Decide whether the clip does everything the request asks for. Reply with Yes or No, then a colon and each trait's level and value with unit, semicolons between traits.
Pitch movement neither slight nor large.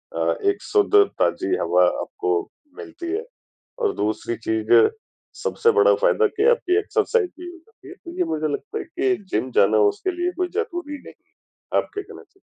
Yes: average, 4.1 semitones